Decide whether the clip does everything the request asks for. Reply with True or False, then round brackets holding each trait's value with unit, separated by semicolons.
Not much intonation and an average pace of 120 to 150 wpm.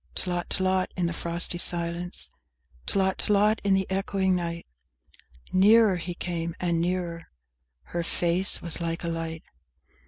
True (2.0 semitones; 145 wpm)